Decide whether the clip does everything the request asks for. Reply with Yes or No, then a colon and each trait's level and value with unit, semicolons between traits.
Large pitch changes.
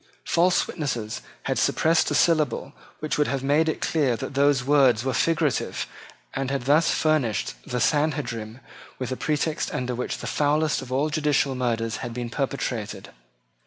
No: average, 3.6 semitones